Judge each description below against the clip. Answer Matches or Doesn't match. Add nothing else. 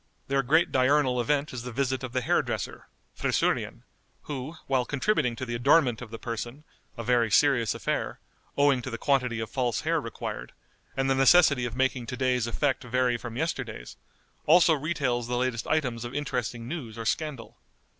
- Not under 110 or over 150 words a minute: Doesn't match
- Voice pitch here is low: Matches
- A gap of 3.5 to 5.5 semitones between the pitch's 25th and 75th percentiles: Doesn't match